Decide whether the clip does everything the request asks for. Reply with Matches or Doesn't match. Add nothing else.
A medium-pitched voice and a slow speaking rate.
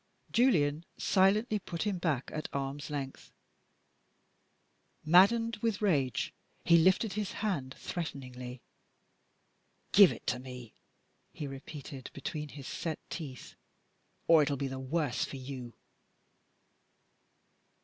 Matches